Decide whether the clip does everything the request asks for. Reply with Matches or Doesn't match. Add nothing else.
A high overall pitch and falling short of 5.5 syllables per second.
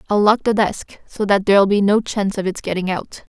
Doesn't match